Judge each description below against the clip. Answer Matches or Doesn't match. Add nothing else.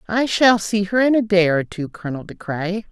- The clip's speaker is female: Matches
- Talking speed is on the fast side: Matches